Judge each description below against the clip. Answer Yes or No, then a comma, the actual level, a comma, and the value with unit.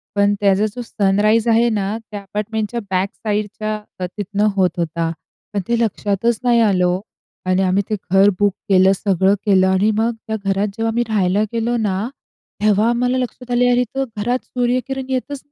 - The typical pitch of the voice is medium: No, high, 210 Hz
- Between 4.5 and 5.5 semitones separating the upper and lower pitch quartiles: No, average, 3.3 semitones